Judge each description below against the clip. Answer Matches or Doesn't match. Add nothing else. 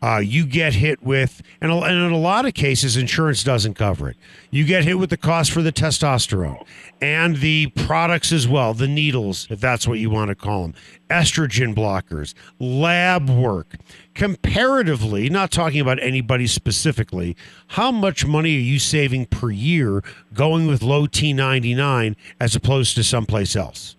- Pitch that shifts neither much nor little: Doesn't match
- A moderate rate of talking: Matches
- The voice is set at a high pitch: Doesn't match